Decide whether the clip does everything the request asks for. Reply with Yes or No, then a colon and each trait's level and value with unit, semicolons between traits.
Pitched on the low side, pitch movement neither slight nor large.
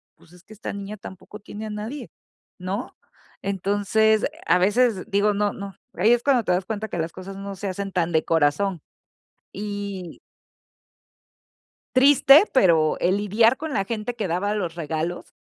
No: high, 200 Hz; average, 3.0 semitones